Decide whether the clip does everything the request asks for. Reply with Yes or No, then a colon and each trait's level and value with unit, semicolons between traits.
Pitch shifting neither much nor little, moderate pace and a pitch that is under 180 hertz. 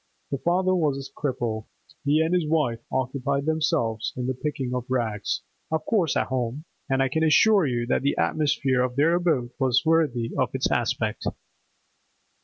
Yes: average, 4.1 semitones; average, 165 wpm; medium, 140 Hz